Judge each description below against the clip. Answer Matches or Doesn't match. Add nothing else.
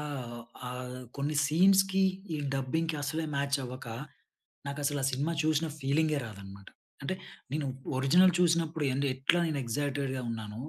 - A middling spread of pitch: Matches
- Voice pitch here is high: Doesn't match